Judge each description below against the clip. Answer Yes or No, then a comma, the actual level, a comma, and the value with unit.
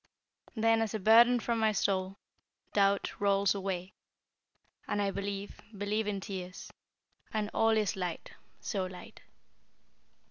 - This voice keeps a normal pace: No, slow, 130 wpm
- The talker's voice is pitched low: No, high, 200 Hz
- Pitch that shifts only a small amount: Yes, narrow, 2.1 semitones